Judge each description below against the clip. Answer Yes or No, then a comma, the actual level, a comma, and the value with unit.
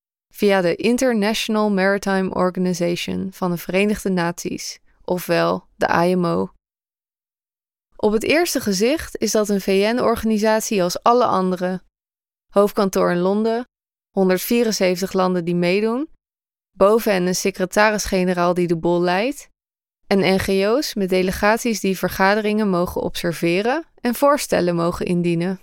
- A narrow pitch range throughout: No, average, 3.1 semitones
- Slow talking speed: Yes, slow, 115 wpm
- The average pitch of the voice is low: No, high, 195 Hz